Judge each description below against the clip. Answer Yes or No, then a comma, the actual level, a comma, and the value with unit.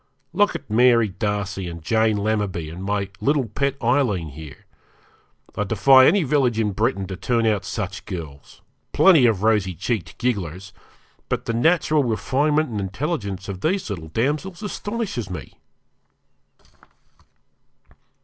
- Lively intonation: Yes, wide, 5.9 semitones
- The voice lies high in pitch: No, low, 110 Hz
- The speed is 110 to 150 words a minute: Yes, slow, 135 wpm